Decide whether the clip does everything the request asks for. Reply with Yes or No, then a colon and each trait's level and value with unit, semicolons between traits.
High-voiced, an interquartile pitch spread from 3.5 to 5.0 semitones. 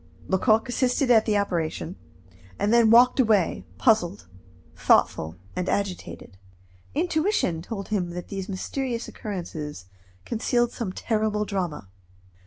Yes: high, 210 Hz; average, 4.7 semitones